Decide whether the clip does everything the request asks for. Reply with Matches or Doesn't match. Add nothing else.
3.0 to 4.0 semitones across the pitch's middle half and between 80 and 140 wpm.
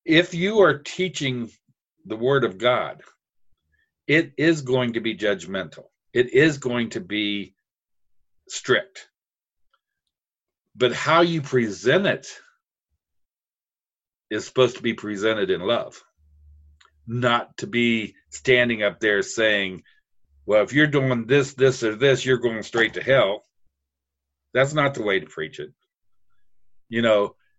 Doesn't match